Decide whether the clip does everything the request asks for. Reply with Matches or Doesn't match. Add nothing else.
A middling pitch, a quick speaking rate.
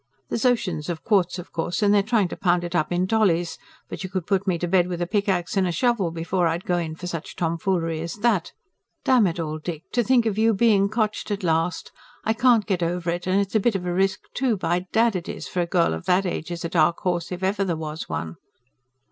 Matches